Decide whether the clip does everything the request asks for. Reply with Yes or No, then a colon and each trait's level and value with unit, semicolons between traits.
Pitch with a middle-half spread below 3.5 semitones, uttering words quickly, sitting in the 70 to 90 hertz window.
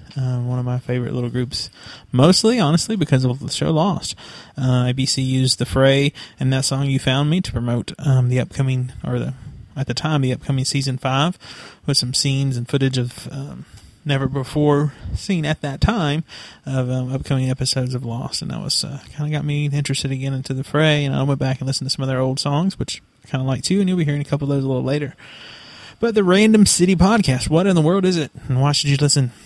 No: narrow, 2.5 semitones; fast, 235 wpm; low, 135 Hz